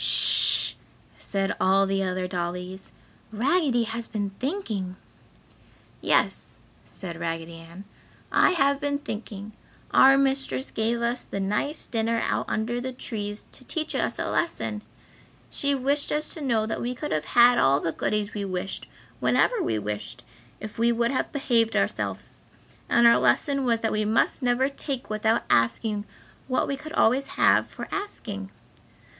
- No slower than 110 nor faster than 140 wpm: No, average, 155 wpm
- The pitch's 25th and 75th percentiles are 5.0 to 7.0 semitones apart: Yes, average, 5.3 semitones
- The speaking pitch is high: Yes, high, 225 Hz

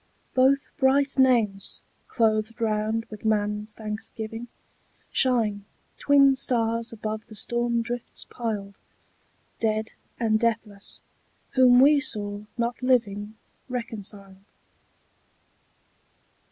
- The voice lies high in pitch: Yes, high, 225 Hz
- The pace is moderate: No, slow, 90 wpm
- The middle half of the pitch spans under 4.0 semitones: Yes, narrow, 2.6 semitones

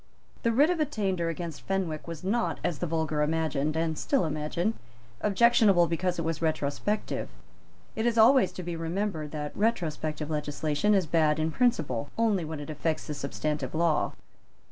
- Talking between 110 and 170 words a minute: Yes, average, 165 wpm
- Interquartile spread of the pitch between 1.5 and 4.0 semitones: No, average, 4.8 semitones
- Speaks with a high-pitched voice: No, medium, 165 Hz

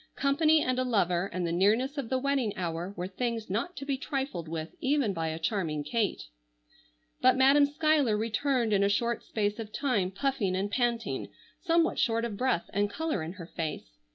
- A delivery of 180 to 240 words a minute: Yes, average, 190 wpm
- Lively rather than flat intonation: Yes, wide, 6.6 semitones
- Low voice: No, high, 225 Hz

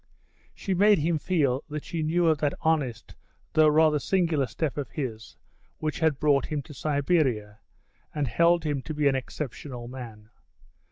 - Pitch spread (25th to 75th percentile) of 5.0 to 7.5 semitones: No, average, 3.5 semitones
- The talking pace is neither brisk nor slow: Yes, average, 165 wpm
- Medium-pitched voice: Yes, medium, 150 Hz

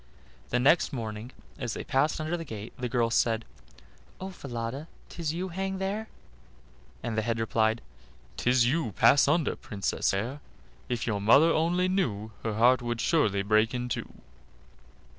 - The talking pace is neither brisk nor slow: Yes, average, 160 wpm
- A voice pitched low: Yes, low, 125 Hz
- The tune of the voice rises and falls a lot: Yes, wide, 6.2 semitones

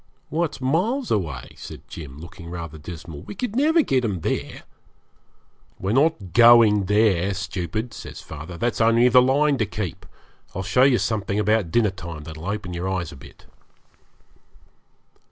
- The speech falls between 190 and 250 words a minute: No, average, 160 wpm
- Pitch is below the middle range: Yes, low, 105 Hz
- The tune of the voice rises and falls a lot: Yes, wide, 6.4 semitones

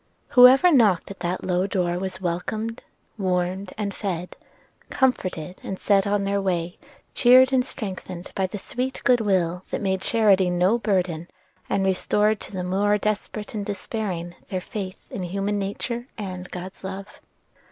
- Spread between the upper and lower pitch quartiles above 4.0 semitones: No, average, 2.7 semitones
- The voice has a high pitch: Yes, high, 195 Hz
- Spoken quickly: No, average, 155 wpm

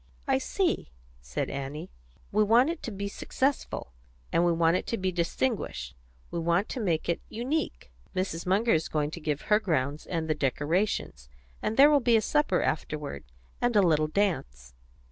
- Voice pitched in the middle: Yes, medium, 170 Hz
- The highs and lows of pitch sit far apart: Yes, wide, 6.1 semitones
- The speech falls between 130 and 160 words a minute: No, average, 180 wpm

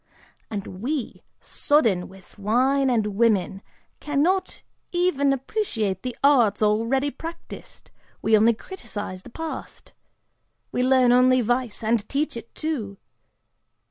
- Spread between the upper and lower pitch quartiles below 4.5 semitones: No, average, 4.9 semitones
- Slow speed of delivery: Yes, slow, 115 wpm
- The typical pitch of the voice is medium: No, high, 245 Hz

